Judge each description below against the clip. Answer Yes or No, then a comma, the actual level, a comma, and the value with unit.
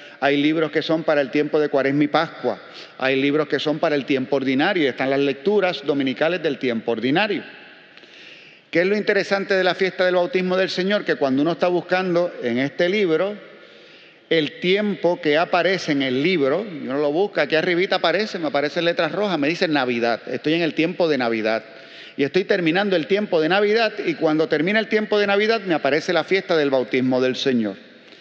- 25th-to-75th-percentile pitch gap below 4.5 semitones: No, average, 5.0 semitones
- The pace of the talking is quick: Yes, fast, 200 wpm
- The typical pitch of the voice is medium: Yes, medium, 160 Hz